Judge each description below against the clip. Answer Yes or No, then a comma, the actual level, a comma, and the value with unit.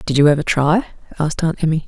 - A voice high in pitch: No, medium, 155 Hz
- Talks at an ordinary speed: No, fast, 225 wpm